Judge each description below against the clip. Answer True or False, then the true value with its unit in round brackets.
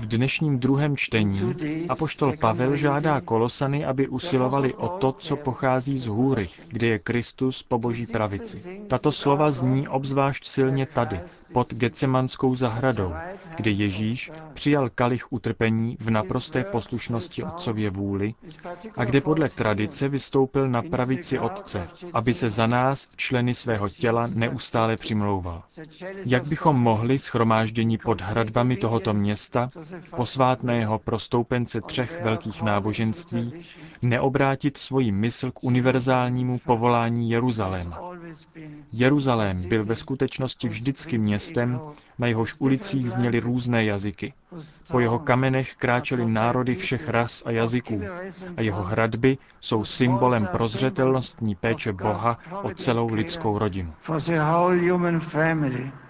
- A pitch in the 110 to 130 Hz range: True (125 Hz)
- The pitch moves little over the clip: False (3.2 semitones)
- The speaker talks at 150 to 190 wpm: False (120 wpm)